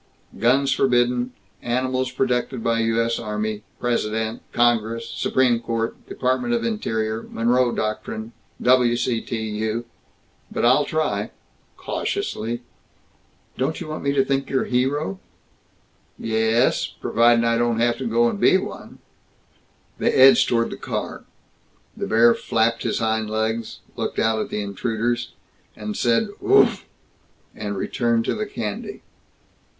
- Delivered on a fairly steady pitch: Yes, narrow, 2.2 semitones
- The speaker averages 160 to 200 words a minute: No, slow, 135 wpm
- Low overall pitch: Yes, low, 115 Hz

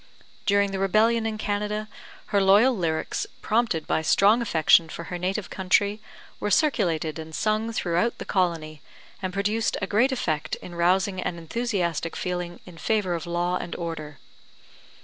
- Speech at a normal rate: Yes, average, 155 wpm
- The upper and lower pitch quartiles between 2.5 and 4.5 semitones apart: Yes, average, 3.9 semitones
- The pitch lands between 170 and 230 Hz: Yes, high, 190 Hz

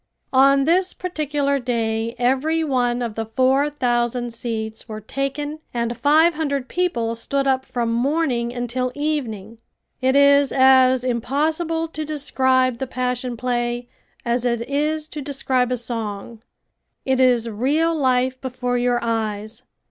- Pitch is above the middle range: Yes, very high, 255 Hz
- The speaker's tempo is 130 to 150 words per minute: Yes, average, 140 wpm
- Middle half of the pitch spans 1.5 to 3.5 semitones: Yes, average, 3.0 semitones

